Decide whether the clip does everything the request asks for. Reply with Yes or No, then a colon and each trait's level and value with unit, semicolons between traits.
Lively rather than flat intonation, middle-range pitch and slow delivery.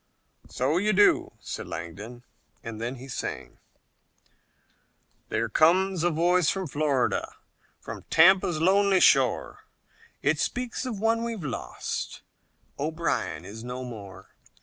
Yes: wide, 7.6 semitones; medium, 160 Hz; slow, 120 wpm